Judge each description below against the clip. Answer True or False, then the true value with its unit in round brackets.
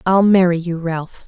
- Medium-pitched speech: True (175 Hz)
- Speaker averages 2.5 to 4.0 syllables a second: False (4.4 syllables/s)